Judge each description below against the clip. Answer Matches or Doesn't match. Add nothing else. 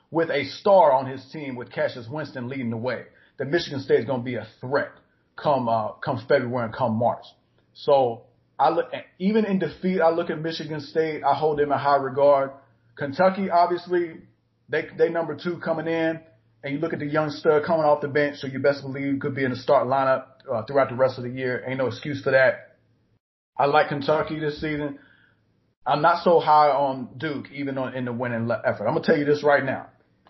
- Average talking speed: Doesn't match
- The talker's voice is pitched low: Doesn't match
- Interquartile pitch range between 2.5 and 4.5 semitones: Matches